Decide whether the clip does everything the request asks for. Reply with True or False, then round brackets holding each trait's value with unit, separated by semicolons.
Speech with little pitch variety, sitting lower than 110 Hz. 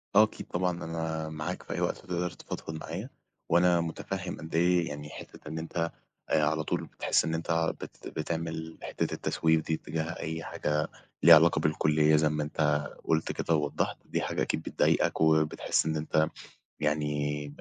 True (1.4 semitones; 80 Hz)